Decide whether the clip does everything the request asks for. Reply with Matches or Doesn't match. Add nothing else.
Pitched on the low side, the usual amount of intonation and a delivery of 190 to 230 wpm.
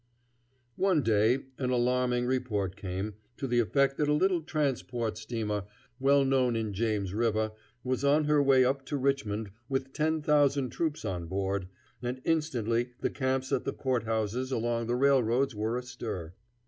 Doesn't match